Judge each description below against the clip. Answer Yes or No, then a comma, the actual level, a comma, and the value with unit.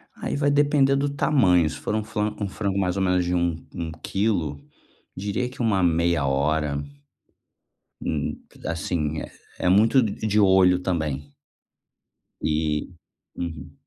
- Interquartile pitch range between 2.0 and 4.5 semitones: No, average, 5.1 semitones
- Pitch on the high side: No, very low, 90 Hz